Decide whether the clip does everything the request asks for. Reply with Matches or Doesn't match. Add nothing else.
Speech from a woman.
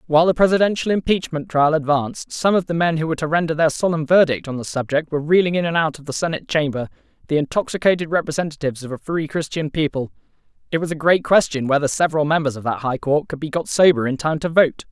Doesn't match